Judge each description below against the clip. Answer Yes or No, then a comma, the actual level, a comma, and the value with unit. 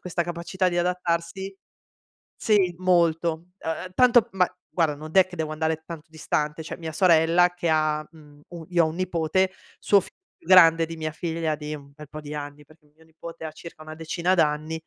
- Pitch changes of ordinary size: No, narrow, 2.3 semitones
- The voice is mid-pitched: Yes, medium, 165 Hz